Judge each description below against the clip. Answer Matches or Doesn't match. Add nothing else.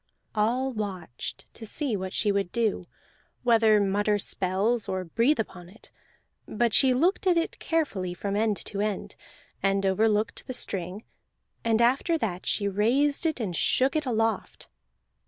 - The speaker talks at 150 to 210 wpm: Matches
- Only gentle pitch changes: Doesn't match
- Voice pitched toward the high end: Matches